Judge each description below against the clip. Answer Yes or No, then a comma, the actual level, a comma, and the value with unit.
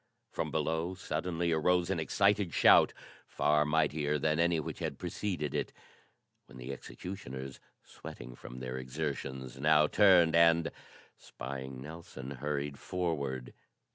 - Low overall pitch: Yes, very low, 75 Hz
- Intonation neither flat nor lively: Yes, average, 4.1 semitones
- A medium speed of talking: No, slow, 125 wpm